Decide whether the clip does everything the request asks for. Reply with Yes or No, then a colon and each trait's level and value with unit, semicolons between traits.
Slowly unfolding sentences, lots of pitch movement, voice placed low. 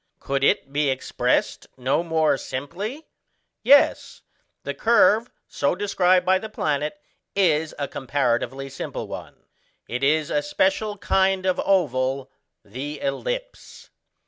No: slow, 120 wpm; wide, 5.9 semitones; medium, 155 Hz